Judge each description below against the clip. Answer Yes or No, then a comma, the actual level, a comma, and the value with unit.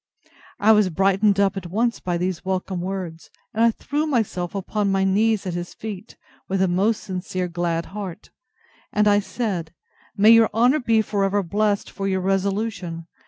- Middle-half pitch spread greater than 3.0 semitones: No, average, 2.7 semitones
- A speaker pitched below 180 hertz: No, high, 195 Hz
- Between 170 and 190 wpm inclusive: Yes, average, 175 wpm